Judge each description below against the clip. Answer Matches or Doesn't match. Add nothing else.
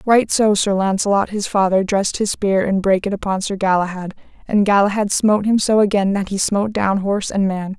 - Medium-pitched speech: Doesn't match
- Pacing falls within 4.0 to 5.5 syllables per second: Doesn't match